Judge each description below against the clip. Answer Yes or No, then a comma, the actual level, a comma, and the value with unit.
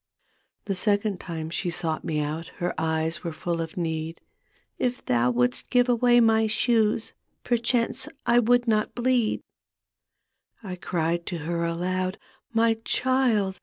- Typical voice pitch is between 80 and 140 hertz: No, medium, 185 Hz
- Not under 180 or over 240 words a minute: No, average, 150 wpm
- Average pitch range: No, wide, 5.9 semitones